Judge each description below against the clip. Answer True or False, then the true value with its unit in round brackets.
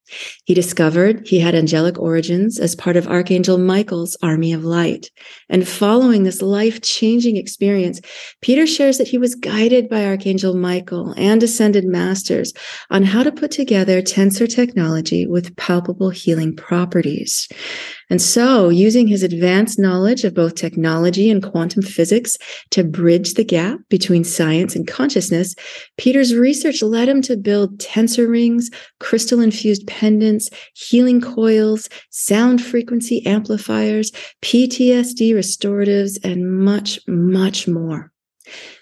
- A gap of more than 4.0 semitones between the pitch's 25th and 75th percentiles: True (4.7 semitones)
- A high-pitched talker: True (200 Hz)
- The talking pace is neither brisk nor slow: False (130 wpm)